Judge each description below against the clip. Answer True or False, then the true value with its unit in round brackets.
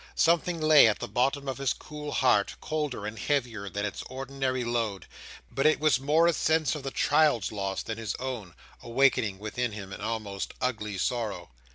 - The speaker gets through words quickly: False (185 wpm)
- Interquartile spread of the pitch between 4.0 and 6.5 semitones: True (5.2 semitones)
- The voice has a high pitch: False (125 Hz)